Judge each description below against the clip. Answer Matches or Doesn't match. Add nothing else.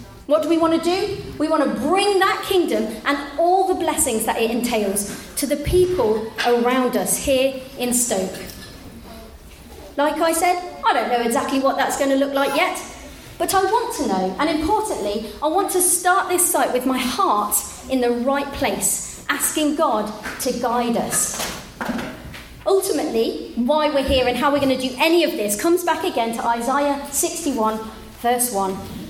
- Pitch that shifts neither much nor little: Doesn't match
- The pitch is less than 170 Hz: Doesn't match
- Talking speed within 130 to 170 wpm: Doesn't match